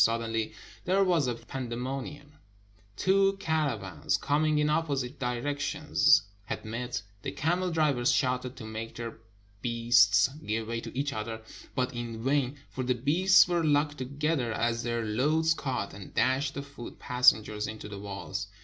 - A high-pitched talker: No, low, 125 Hz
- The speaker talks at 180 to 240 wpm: No, average, 160 wpm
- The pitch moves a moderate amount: Yes, average, 4.4 semitones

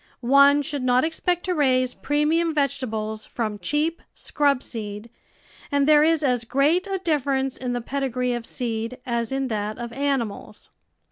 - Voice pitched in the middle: No, very high, 265 Hz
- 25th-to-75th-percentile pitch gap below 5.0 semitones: Yes, average, 3.9 semitones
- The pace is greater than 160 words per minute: No, average, 155 wpm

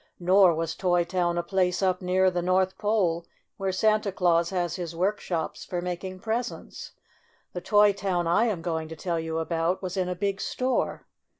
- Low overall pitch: No, medium, 180 Hz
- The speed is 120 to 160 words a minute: No, average, 185 wpm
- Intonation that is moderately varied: No, narrow, 2.1 semitones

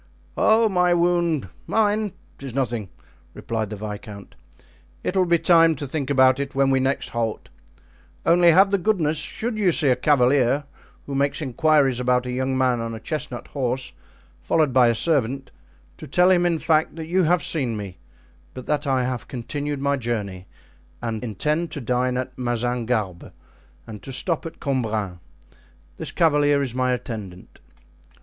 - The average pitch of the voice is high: No, low, 135 Hz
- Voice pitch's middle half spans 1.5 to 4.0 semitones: No, average, 5.0 semitones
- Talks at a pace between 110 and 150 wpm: No, average, 160 wpm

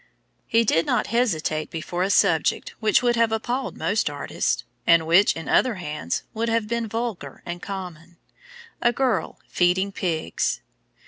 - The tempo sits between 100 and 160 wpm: Yes, average, 150 wpm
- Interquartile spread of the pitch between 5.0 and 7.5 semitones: Yes, wide, 5.5 semitones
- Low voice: No, high, 200 Hz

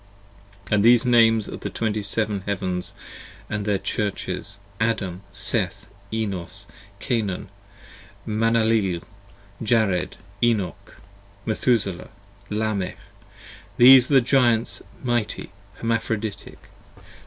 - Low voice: Yes, low, 110 Hz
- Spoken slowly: Yes, slow, 95 wpm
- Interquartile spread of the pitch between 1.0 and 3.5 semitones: Yes, narrow, 2.5 semitones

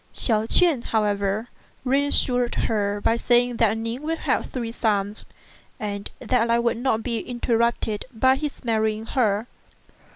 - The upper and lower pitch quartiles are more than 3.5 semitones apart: No, narrow, 2.4 semitones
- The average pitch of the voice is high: Yes, high, 230 Hz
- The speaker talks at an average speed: Yes, average, 155 wpm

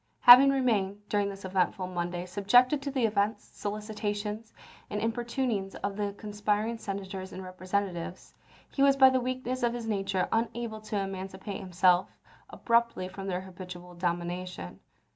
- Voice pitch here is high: Yes, high, 205 Hz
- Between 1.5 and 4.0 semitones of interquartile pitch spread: Yes, average, 3.6 semitones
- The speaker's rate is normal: Yes, average, 145 wpm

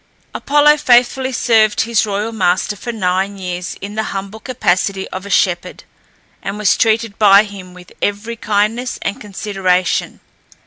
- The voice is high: Yes, high, 205 Hz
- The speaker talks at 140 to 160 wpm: Yes, average, 145 wpm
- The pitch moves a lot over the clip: No, average, 2.8 semitones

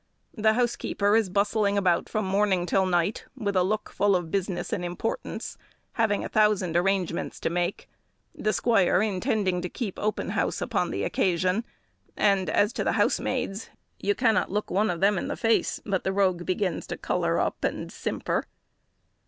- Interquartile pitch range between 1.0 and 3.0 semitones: Yes, average, 2.7 semitones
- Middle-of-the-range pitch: No, high, 195 Hz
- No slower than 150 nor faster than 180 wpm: Yes, average, 175 wpm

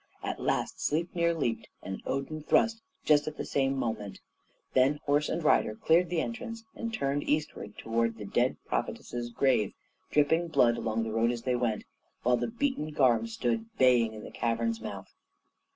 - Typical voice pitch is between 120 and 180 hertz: Yes, low, 135 Hz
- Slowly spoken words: No, average, 170 wpm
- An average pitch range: No, wide, 5.8 semitones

